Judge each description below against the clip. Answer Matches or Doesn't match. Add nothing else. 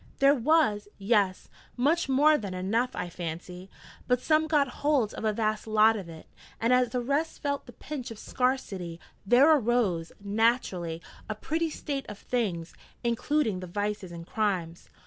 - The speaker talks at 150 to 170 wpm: Matches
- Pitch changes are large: Matches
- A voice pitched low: Doesn't match